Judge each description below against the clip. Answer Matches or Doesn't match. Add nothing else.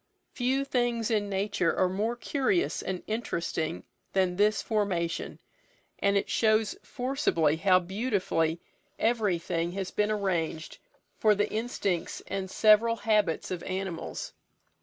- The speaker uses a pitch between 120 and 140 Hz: Doesn't match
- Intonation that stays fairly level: Doesn't match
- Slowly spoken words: Matches